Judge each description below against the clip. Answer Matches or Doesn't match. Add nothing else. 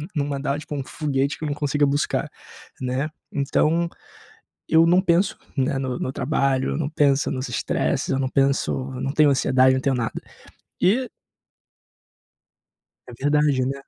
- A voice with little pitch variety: Matches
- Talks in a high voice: Doesn't match